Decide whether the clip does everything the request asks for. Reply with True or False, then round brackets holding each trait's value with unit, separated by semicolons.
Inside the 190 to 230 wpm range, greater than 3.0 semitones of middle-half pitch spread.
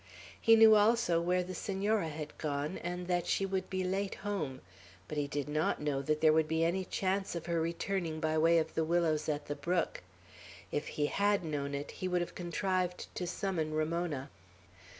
True (195 wpm; 3.4 semitones)